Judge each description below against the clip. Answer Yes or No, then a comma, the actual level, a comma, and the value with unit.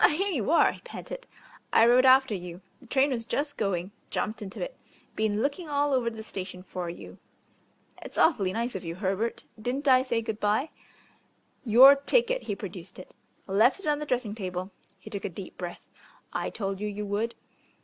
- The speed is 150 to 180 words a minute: No, average, 195 wpm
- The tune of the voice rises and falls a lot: Yes, wide, 5.7 semitones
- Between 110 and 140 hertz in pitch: No, high, 225 Hz